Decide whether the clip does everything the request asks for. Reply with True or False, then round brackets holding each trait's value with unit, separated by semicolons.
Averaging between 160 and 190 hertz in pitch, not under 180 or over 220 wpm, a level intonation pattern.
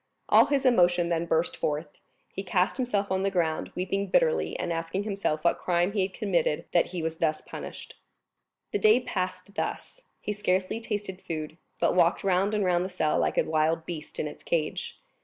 False (185 Hz; 195 wpm; 3.2 semitones)